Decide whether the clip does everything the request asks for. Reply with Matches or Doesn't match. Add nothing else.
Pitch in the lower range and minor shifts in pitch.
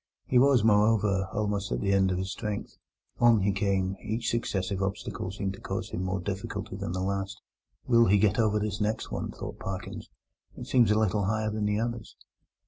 Matches